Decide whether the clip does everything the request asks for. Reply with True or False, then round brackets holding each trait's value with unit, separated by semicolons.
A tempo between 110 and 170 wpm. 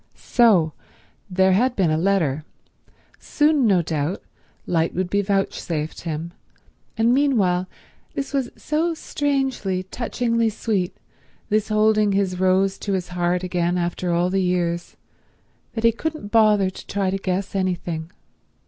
True (140 wpm)